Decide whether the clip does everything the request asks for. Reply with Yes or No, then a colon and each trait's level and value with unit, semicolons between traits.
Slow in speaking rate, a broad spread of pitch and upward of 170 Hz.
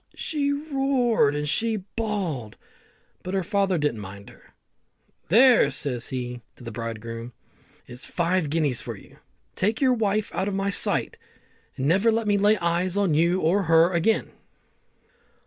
No: average, 155 wpm; wide, 6.9 semitones; medium, 185 Hz